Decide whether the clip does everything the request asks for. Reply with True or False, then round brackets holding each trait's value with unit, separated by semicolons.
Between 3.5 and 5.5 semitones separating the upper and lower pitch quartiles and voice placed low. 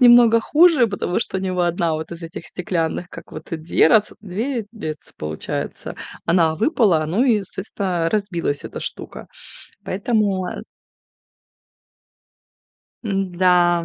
False (4.4 semitones; 185 Hz)